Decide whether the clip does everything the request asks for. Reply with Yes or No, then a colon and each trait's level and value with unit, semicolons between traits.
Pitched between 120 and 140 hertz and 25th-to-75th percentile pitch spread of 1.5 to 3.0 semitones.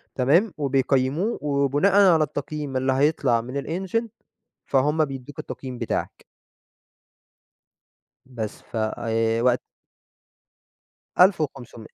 No: low, 135 Hz; average, 3.4 semitones